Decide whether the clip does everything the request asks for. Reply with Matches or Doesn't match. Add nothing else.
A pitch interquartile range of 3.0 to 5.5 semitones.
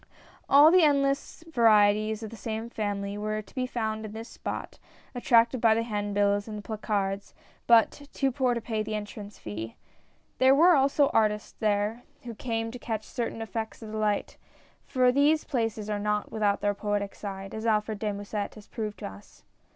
Doesn't match